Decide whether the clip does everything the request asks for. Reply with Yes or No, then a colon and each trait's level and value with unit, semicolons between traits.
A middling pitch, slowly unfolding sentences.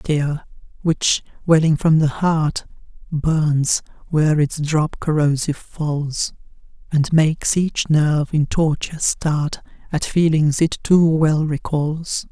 Yes: medium, 155 Hz; slow, 125 wpm